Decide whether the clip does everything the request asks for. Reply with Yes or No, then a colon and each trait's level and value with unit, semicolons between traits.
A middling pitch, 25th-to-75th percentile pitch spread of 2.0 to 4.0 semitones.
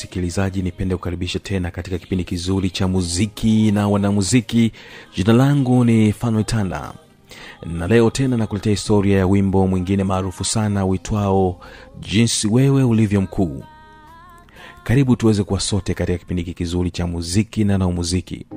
No: low, 100 Hz; average, 3.1 semitones